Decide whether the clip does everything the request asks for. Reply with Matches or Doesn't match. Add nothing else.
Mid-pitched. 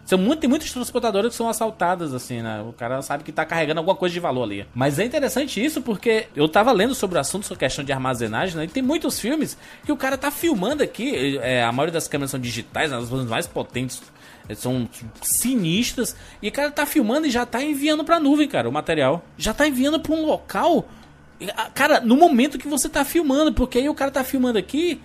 Doesn't match